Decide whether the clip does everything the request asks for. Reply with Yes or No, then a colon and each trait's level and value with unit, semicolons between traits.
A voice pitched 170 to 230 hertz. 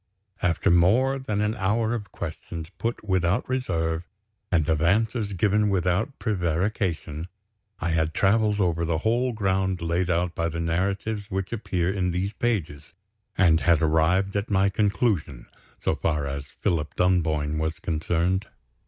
No: very low, 90 Hz